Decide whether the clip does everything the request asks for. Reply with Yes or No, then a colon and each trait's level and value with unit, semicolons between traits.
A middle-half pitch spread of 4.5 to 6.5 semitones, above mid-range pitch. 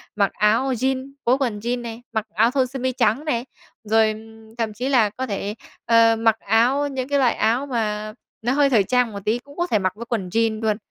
No: average, 3.0 semitones; high, 230 Hz